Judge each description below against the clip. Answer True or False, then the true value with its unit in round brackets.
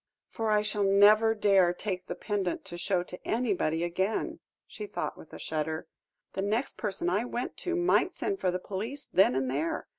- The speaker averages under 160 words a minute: False (190 wpm)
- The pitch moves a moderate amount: True (3.8 semitones)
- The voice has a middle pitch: False (195 Hz)